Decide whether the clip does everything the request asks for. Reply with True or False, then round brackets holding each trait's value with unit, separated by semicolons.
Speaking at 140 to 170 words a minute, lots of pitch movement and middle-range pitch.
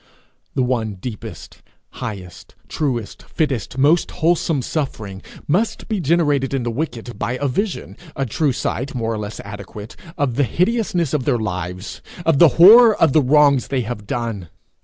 False (160 wpm; 6.0 semitones; 130 Hz)